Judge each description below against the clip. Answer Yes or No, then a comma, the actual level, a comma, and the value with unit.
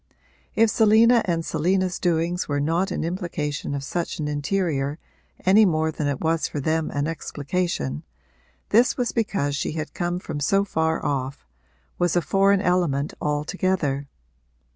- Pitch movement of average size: Yes, average, 4.3 semitones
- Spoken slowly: No, average, 150 wpm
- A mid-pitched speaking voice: Yes, medium, 165 Hz